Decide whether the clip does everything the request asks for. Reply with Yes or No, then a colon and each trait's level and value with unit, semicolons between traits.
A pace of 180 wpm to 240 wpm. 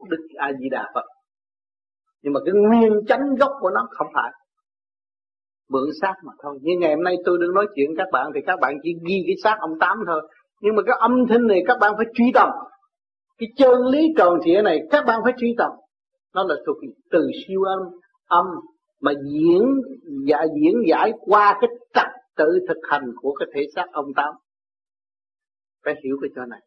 Yes: average, 210 wpm